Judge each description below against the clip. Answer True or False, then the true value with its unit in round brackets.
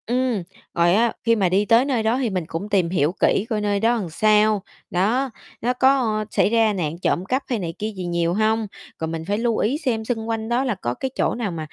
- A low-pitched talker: False (215 Hz)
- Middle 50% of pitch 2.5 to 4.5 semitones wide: True (4.2 semitones)